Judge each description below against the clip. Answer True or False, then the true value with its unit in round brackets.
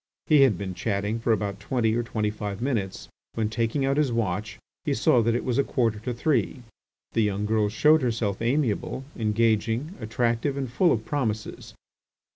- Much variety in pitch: False (3.4 semitones)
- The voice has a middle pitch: False (115 Hz)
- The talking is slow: False (180 wpm)